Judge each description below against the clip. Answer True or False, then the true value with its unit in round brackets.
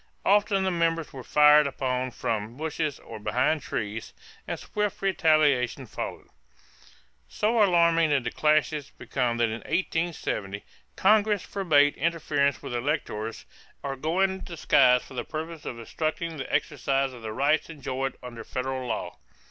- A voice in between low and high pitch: True (145 Hz)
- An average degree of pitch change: True (5.0 semitones)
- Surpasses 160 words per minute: False (145 wpm)